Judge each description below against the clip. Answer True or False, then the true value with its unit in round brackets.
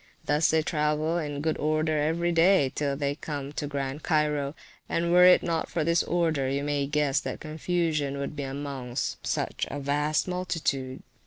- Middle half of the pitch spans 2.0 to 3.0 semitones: True (2.5 semitones)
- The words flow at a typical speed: True (175 wpm)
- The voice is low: False (150 Hz)